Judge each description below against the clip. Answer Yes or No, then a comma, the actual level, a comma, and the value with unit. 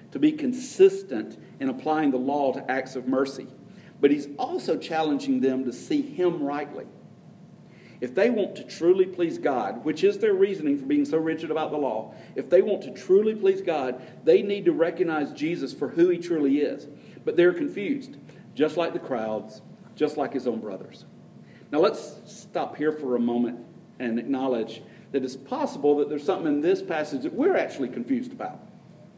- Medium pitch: Yes, medium, 165 Hz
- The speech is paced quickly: No, average, 185 wpm